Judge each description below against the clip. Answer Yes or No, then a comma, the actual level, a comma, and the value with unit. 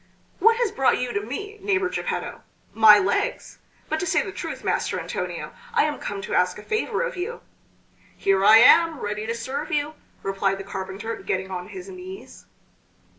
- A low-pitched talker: No, very high, 250 Hz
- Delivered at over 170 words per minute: Yes, average, 180 wpm